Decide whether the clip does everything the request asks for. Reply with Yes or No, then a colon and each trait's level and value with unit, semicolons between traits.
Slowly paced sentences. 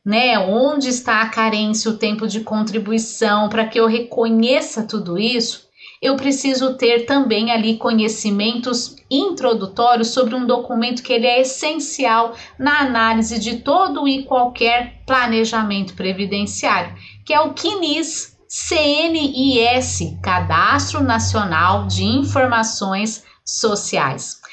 Yes: slow, 115 wpm